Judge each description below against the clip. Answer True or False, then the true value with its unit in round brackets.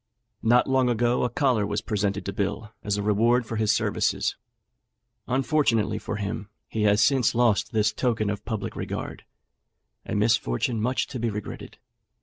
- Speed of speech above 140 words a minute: True (160 wpm)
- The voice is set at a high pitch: False (110 Hz)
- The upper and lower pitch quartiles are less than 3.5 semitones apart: True (2.8 semitones)